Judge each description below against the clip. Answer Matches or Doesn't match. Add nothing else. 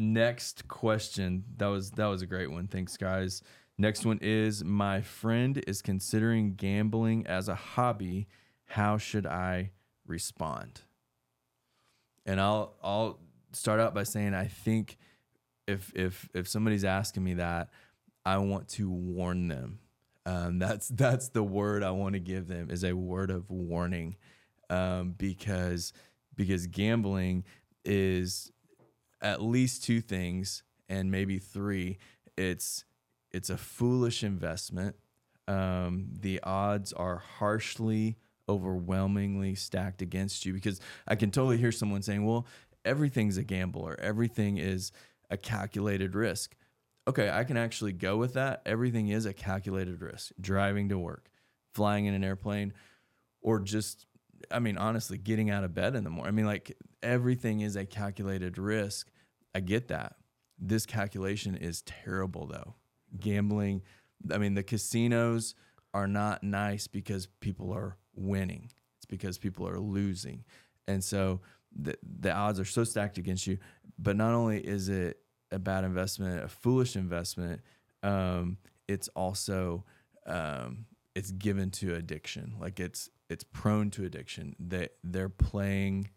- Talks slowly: Doesn't match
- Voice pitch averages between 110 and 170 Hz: Doesn't match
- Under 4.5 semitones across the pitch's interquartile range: Matches